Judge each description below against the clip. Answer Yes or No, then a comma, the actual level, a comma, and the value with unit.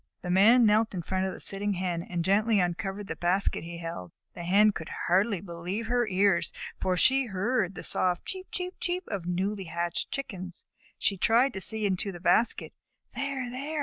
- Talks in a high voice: Yes, high, 195 Hz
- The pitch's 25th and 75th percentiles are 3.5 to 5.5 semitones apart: Yes, average, 4.2 semitones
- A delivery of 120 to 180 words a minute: No, average, 190 wpm